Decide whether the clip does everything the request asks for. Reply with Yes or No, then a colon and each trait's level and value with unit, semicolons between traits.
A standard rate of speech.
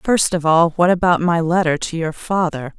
No: fast, 215 wpm